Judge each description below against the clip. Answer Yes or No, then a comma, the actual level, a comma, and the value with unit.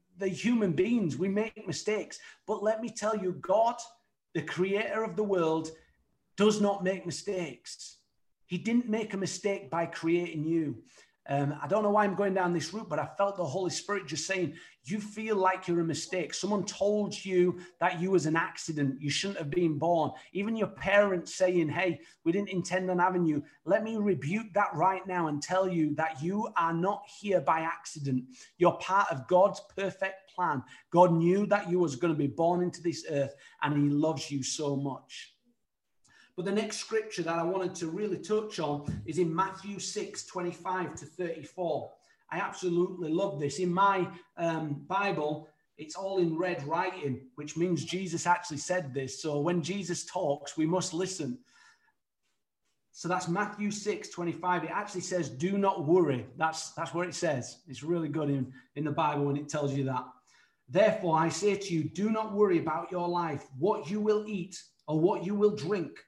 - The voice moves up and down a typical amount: Yes, average, 3.8 semitones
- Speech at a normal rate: Yes, average, 190 wpm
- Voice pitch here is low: No, medium, 180 Hz